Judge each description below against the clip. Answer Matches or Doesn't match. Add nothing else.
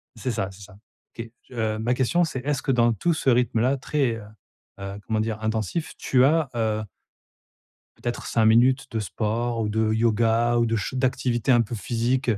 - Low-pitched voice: Matches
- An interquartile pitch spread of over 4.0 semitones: Doesn't match